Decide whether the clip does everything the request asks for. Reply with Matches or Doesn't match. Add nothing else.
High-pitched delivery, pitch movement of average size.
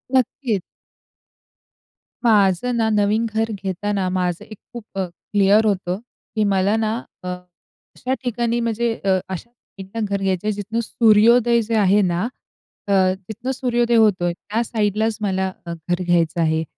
Matches